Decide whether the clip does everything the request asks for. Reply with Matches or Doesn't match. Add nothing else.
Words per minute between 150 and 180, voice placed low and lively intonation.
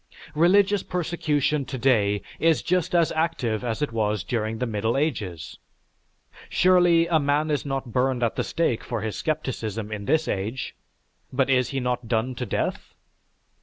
Matches